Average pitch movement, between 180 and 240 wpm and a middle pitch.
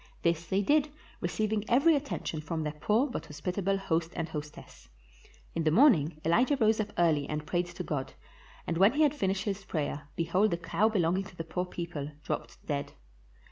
Yes: average, 4.8 semitones; average, 185 wpm; medium, 175 Hz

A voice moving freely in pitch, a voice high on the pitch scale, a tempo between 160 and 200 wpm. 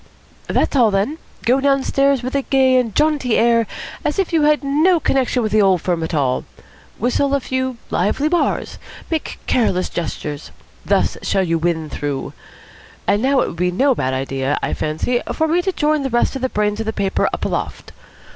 Yes: wide, 7.4 semitones; high, 245 Hz; average, 195 wpm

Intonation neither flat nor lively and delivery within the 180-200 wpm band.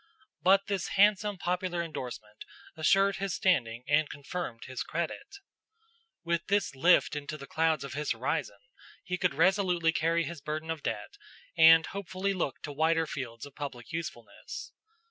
No: average, 4.3 semitones; average, 150 wpm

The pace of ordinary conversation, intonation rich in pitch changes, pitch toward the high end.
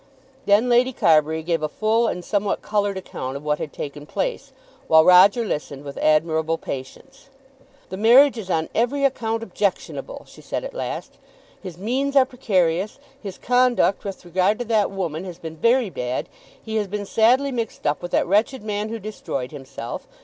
Yes: average, 180 wpm; wide, 6.3 semitones; high, 200 Hz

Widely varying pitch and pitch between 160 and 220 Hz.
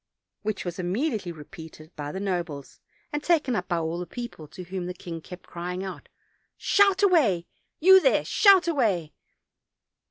Yes: wide, 8.5 semitones; medium, 185 Hz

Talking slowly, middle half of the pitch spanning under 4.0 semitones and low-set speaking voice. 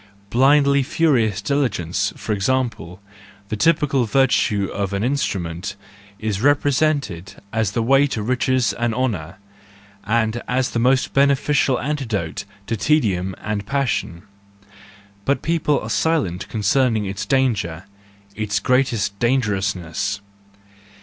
No: slow, 115 wpm; average, 5.2 semitones; low, 115 Hz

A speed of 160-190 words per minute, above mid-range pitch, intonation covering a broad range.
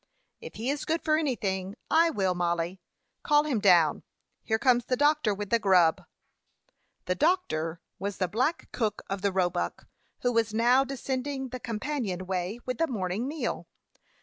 Yes: average, 165 wpm; high, 225 Hz; wide, 6.3 semitones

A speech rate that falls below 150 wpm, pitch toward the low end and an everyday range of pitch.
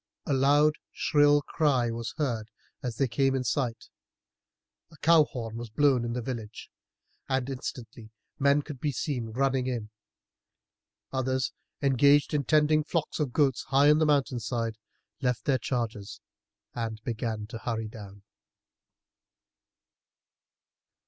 Yes: slow, 135 wpm; low, 130 Hz; average, 3.8 semitones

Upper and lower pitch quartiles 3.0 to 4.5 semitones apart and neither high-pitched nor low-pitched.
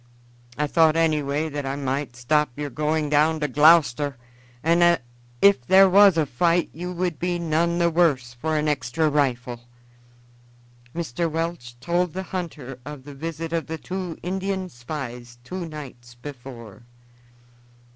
Yes: average, 4.1 semitones; medium, 155 Hz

